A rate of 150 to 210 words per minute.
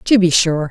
No: fast, 255 wpm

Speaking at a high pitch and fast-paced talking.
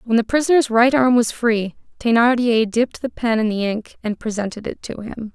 Yes: high, 230 Hz; fast, 215 wpm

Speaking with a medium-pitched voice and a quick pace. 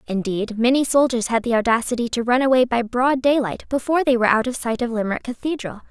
No: high, 245 Hz; fast, 215 wpm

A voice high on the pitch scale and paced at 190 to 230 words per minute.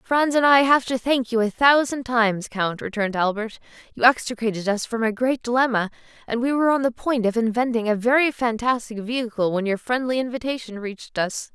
Yes: high, 235 Hz; average, 200 wpm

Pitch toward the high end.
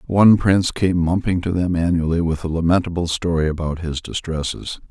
No: very low, 85 Hz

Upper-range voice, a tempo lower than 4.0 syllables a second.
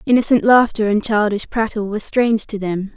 No: high, 215 Hz; 5.7 syllables/s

